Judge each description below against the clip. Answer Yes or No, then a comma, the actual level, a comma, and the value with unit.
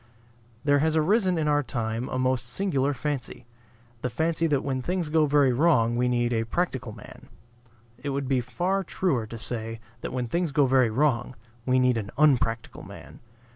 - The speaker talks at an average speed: Yes, average, 180 wpm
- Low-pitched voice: Yes, low, 130 Hz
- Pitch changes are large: No, average, 4.1 semitones